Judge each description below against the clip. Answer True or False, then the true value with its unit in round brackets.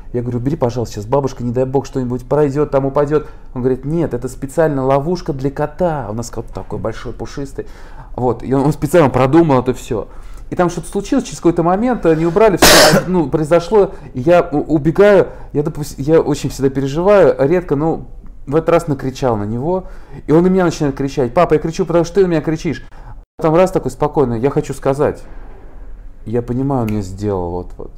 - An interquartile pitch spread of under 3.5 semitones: False (4.7 semitones)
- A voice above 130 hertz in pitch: True (140 Hz)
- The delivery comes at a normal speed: False (195 wpm)